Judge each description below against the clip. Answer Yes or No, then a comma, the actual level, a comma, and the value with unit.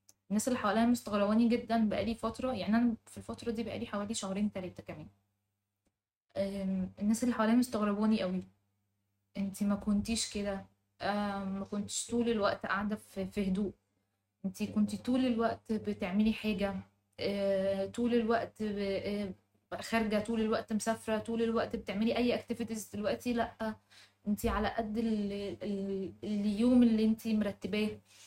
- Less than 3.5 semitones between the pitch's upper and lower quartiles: Yes, narrow, 2.6 semitones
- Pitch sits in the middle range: No, high, 210 Hz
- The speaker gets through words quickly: No, average, 125 wpm